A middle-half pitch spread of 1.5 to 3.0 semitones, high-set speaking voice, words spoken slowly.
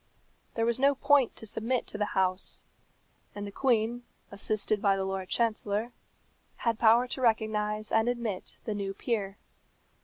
No: average, 2.7 semitones; high, 220 Hz; average, 155 wpm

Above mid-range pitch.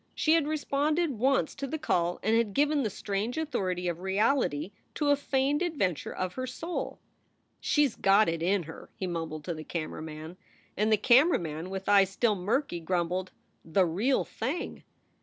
Yes: high, 205 Hz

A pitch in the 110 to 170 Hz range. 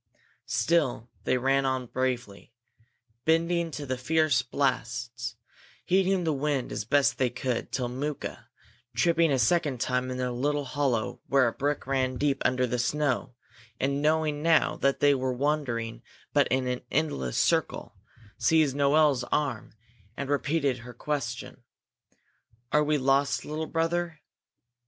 Yes: low, 135 Hz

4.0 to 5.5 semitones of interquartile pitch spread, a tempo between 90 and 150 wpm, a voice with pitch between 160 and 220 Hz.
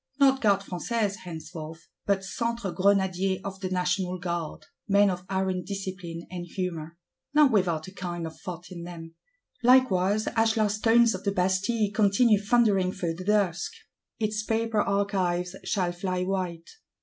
No: average, 2.9 semitones; average, 145 wpm; high, 190 Hz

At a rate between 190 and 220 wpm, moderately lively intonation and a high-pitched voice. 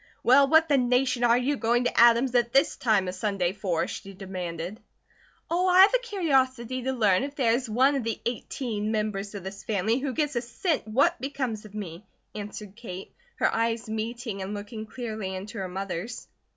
Yes: average, 195 wpm; average, 4.3 semitones; high, 230 Hz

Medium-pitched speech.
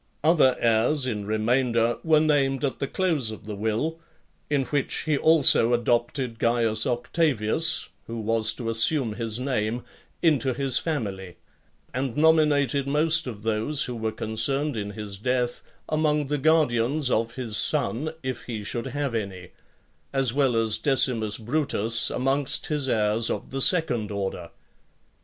No: low, 125 Hz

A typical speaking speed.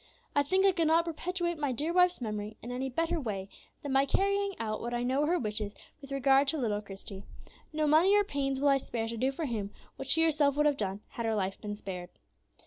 No: fast, 240 wpm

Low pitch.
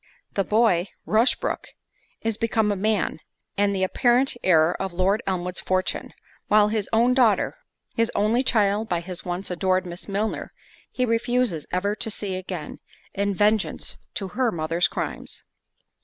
No: high, 200 Hz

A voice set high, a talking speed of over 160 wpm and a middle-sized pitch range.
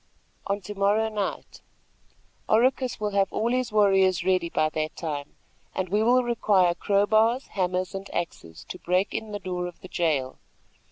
Yes: high, 195 Hz; average, 170 wpm; average, 3.3 semitones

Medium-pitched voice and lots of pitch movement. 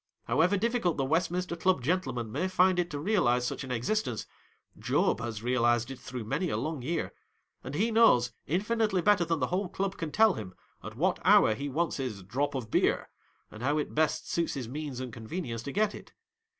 Yes: medium, 150 Hz; wide, 7.0 semitones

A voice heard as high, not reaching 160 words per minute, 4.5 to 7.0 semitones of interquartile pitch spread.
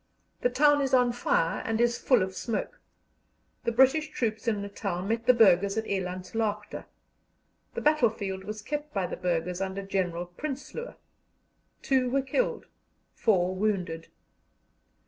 Yes: high, 215 Hz; average, 145 wpm; average, 5.0 semitones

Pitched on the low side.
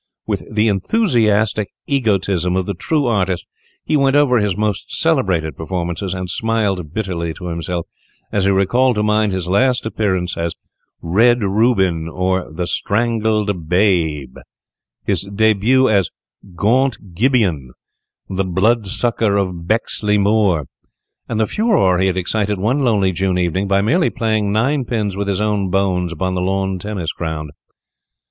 Yes: low, 100 Hz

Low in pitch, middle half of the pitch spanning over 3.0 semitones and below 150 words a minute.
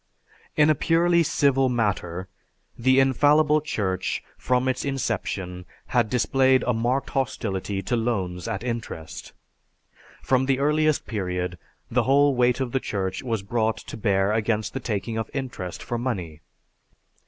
Yes: low, 120 Hz; average, 5.1 semitones; average, 140 wpm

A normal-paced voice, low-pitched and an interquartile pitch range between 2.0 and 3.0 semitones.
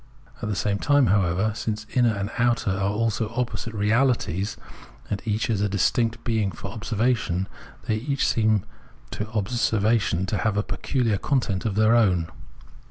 Yes: average, 165 wpm; low, 110 Hz; narrow, 2.6 semitones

